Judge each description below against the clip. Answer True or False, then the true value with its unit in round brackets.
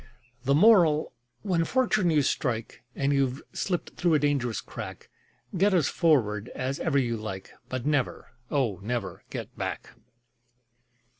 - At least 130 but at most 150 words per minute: True (140 wpm)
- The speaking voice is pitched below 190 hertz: True (140 Hz)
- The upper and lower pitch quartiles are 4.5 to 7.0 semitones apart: True (5.3 semitones)